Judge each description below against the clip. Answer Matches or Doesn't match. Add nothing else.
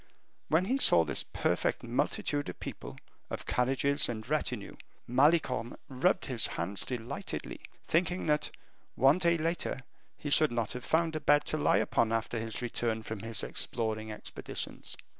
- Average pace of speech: Matches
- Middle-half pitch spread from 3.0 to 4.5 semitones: Doesn't match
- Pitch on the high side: Doesn't match